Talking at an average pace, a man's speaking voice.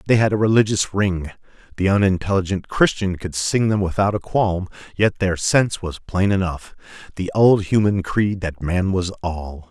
Yes: average, 165 wpm; male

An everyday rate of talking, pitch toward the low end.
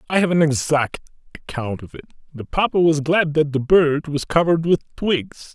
No: average, 195 wpm; medium, 150 Hz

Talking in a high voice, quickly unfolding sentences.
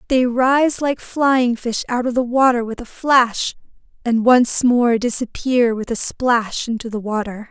No: high, 240 Hz; average, 175 wpm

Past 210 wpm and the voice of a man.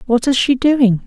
No: fast, 225 wpm; female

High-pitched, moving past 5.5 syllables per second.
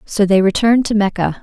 Yes: high, 205 Hz; 6.1 syllables/s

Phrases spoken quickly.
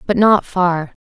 No: average, 175 wpm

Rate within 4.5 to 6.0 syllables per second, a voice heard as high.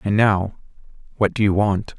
No: 4.7 syllables/s; low, 100 Hz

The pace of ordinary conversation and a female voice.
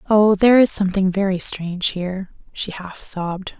Yes: average, 165 wpm; female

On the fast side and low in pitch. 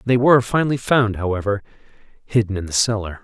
No: average, 165 wpm; low, 110 Hz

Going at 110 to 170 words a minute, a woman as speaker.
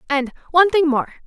Yes: average, 140 wpm; female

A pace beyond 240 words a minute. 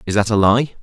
Yes: fast, 290 wpm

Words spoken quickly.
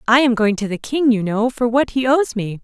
Yes: fast, 295 wpm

